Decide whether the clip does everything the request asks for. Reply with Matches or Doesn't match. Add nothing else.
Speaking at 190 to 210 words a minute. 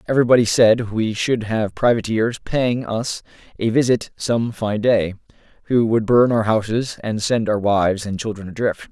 Doesn't match